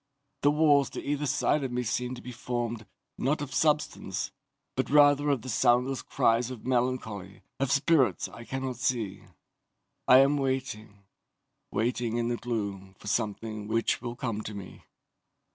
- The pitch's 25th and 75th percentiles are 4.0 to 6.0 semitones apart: No, average, 3.3 semitones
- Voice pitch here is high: No, low, 125 Hz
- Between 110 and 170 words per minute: Yes, average, 160 wpm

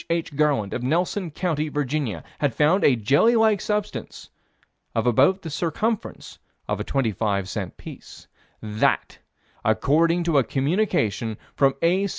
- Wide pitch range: Yes, wide, 6.8 semitones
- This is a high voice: No, medium, 150 Hz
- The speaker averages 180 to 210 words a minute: No, average, 145 wpm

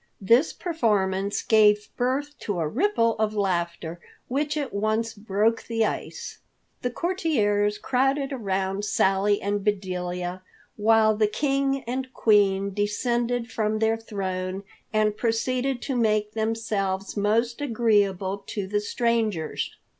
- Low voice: No, high, 215 Hz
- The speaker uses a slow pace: Yes, slow, 125 wpm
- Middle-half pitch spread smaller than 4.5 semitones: Yes, average, 3.1 semitones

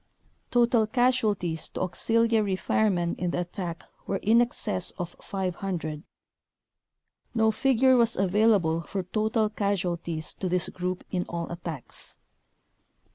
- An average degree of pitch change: Yes, average, 4.2 semitones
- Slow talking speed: Yes, slow, 125 wpm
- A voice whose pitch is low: No, high, 190 Hz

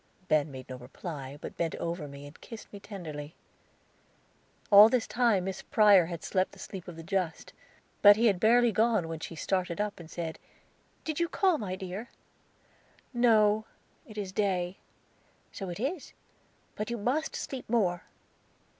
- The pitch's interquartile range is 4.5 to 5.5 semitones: Yes, average, 4.9 semitones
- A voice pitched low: No, high, 195 Hz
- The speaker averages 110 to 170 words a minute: Yes, average, 165 wpm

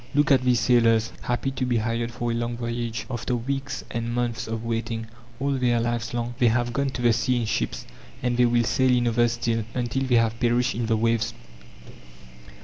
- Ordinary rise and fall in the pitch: No, narrow, 1.2 semitones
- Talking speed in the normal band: No, fast, 210 wpm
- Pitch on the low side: Yes, low, 120 Hz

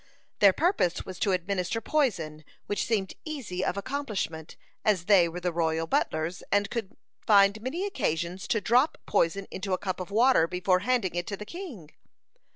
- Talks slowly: No, average, 170 wpm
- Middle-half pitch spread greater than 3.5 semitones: Yes, average, 4.5 semitones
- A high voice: Yes, high, 195 Hz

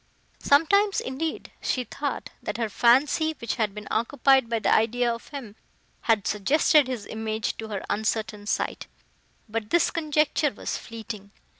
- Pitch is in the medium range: No, high, 235 Hz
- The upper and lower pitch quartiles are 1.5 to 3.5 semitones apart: No, average, 4.7 semitones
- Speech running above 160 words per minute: No, average, 150 wpm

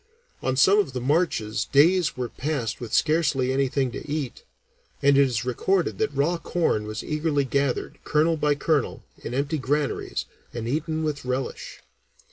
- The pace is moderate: Yes, average, 165 wpm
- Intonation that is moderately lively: Yes, average, 3.6 semitones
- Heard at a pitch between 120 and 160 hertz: Yes, medium, 140 Hz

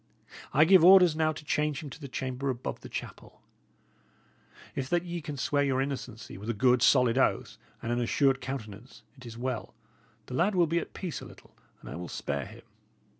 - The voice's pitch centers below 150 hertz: Yes, low, 135 Hz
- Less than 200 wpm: No, fast, 205 wpm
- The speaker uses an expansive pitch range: No, average, 4.2 semitones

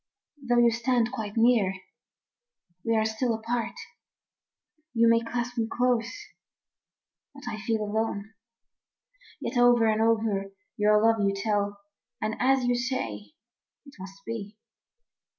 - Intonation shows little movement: Yes, narrow, 2.3 semitones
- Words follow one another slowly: Yes, slow, 130 wpm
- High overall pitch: Yes, high, 225 Hz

